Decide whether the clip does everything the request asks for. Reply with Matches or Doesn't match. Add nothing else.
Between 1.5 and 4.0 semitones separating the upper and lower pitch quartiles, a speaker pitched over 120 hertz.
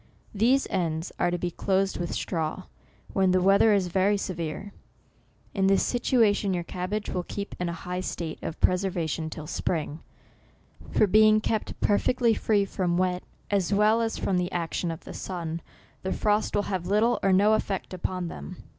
Matches